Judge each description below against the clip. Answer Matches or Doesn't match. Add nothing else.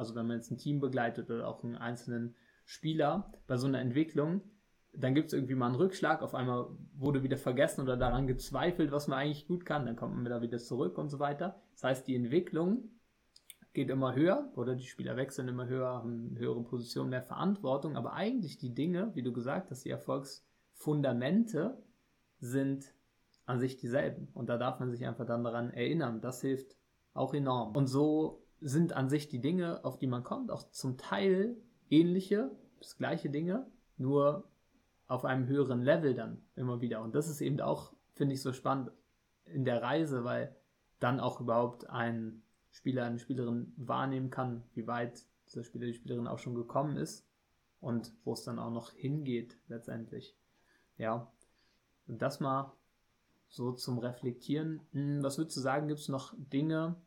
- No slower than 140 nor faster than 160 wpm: Doesn't match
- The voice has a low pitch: Matches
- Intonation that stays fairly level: Doesn't match